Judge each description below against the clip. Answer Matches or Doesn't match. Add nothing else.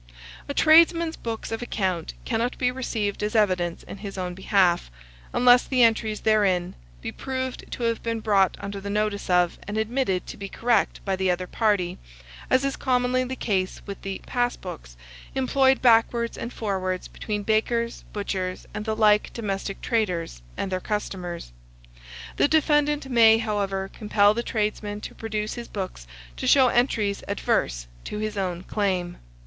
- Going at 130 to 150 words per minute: Doesn't match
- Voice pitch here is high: Matches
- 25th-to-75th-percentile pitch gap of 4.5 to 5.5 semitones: Doesn't match